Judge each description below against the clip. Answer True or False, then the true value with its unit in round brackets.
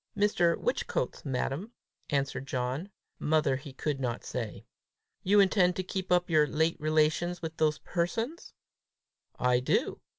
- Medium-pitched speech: True (155 Hz)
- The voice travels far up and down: False (4.8 semitones)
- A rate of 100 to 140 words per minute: True (135 wpm)